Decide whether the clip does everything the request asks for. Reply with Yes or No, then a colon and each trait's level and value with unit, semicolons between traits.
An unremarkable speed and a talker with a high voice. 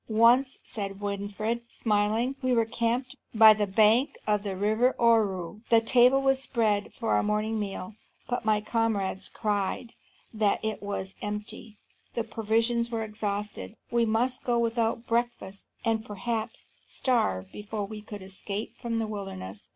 Yes: average, 150 wpm; high, 220 Hz